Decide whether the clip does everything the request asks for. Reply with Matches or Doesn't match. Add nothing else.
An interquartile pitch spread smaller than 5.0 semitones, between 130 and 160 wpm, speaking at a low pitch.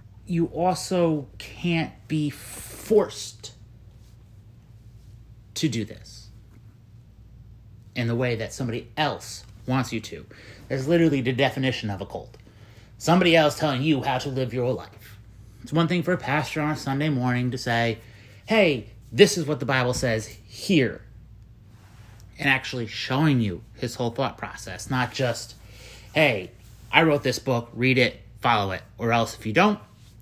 Matches